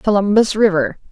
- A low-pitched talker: No, high, 200 Hz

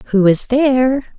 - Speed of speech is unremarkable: Yes, average, 150 wpm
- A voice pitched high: Yes, high, 245 Hz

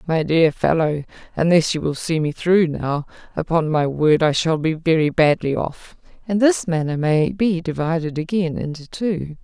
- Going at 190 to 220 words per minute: No, average, 180 wpm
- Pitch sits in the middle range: Yes, medium, 165 Hz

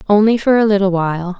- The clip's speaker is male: No, female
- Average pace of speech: No, fast, 215 wpm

